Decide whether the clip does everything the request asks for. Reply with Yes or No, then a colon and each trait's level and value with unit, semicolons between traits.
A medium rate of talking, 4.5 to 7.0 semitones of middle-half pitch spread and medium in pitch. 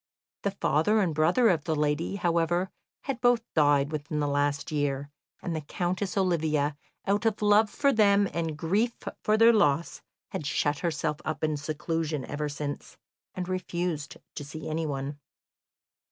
Yes: average, 155 wpm; average, 4.9 semitones; medium, 160 Hz